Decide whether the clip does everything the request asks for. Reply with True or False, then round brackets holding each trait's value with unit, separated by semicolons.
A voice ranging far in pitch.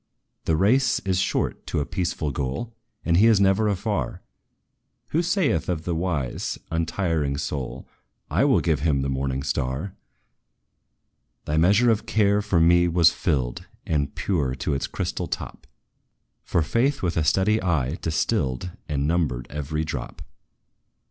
True (5.7 semitones)